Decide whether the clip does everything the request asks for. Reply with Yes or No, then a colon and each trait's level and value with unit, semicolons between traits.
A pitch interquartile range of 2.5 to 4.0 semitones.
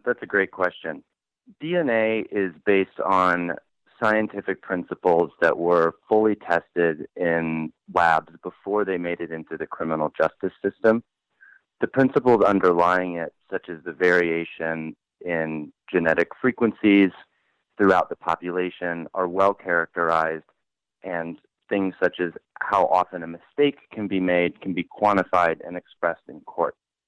Yes: average, 3.1 semitones